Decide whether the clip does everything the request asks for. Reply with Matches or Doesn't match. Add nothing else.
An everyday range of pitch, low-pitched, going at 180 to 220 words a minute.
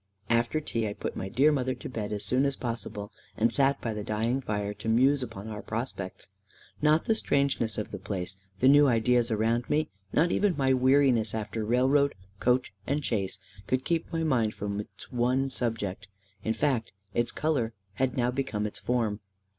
Matches